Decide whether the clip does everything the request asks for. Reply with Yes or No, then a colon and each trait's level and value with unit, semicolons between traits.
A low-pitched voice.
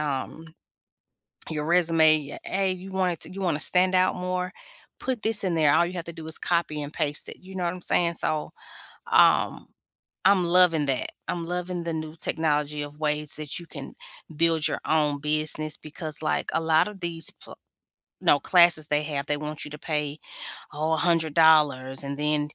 No: medium, 160 Hz